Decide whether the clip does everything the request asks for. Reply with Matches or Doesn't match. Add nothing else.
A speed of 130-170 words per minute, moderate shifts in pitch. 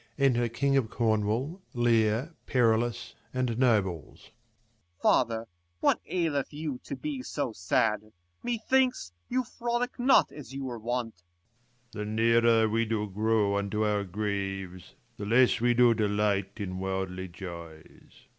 Matches